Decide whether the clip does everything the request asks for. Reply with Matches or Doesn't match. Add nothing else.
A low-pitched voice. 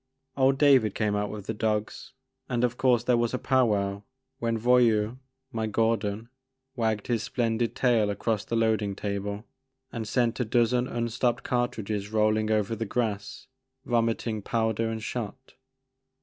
Matches